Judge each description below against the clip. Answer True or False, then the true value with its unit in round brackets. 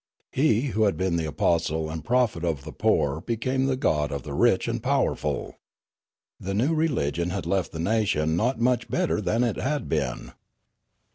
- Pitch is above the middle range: False (100 Hz)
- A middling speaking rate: True (185 wpm)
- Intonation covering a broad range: True (7.4 semitones)